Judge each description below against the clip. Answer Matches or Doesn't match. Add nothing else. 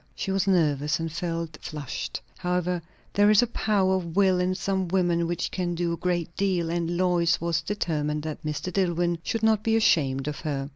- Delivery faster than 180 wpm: Matches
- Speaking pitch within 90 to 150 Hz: Doesn't match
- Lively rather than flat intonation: Doesn't match